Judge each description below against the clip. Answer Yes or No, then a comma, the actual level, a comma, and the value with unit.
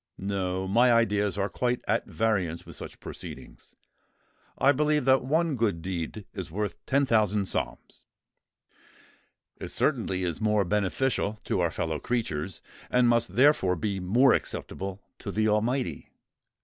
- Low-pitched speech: Yes, low, 105 Hz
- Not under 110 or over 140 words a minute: Yes, slow, 135 wpm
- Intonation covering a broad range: No, average, 4.6 semitones